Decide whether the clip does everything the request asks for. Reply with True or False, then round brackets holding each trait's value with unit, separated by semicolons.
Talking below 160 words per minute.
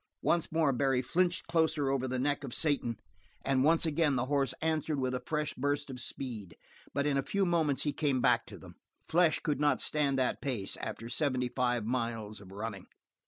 False (200 wpm)